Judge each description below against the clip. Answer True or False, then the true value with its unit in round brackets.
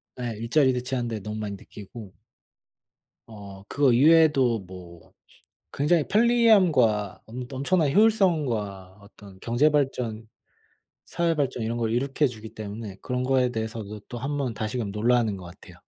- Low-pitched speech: True (120 Hz)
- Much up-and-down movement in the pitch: False (4.8 semitones)